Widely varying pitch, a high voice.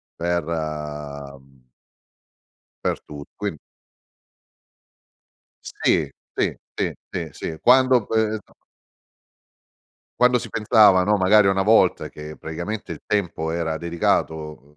No: wide, 5.7 semitones; very low, 85 Hz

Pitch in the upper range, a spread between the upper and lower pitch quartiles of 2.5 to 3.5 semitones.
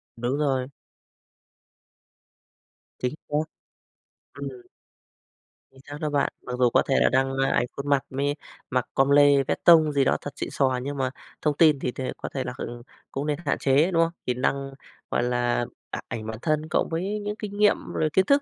No: medium, 140 Hz; average, 2.8 semitones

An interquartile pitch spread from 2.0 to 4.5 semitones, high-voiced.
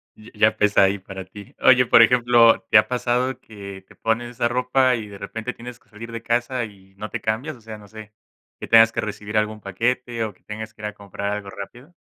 No: average, 2.7 semitones; low, 110 Hz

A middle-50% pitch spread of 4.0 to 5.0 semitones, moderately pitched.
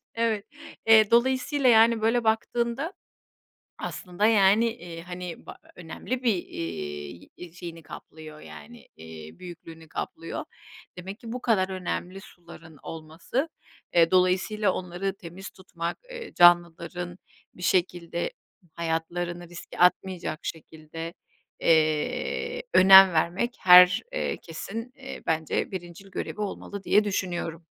Yes: average, 4.4 semitones; medium, 180 Hz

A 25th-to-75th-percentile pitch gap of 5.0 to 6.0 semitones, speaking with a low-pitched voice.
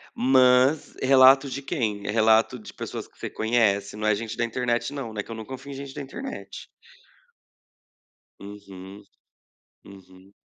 No: average, 4.3 semitones; low, 115 Hz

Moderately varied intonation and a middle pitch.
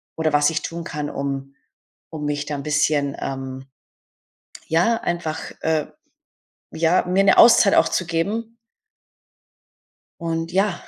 Yes: average, 3.1 semitones; medium, 160 Hz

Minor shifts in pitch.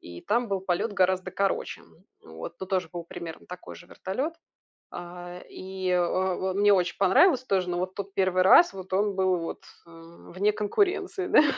Yes: narrow, 2.2 semitones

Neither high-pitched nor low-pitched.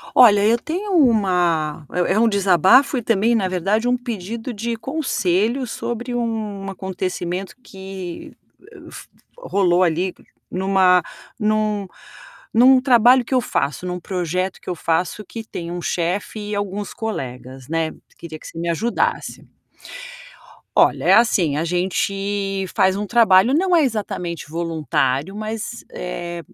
No: high, 195 Hz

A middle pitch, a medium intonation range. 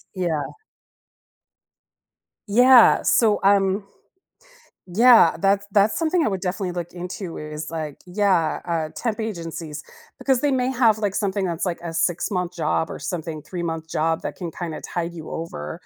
Yes: medium, 180 Hz; average, 4.1 semitones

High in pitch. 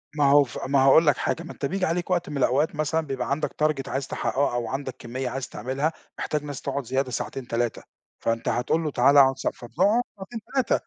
No: medium, 140 Hz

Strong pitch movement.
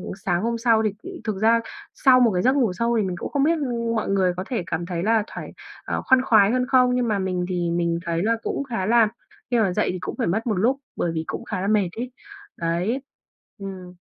No: average, 4.7 semitones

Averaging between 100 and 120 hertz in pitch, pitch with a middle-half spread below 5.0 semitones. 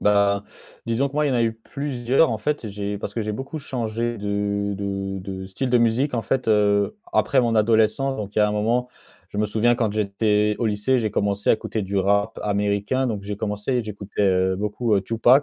Yes: low, 105 Hz; average, 2.8 semitones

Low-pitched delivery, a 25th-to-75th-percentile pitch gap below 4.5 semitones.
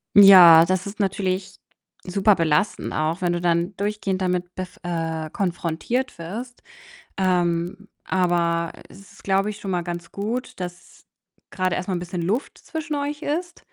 No: medium, 185 Hz; average, 2.8 semitones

